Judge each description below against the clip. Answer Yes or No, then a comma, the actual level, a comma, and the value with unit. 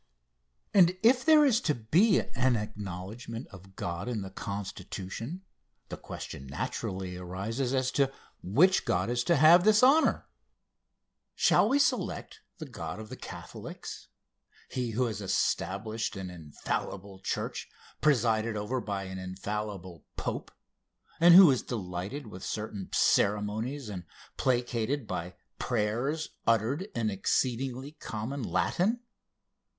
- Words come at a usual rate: No, slow, 125 wpm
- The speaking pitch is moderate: No, low, 115 Hz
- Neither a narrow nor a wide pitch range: No, wide, 6.2 semitones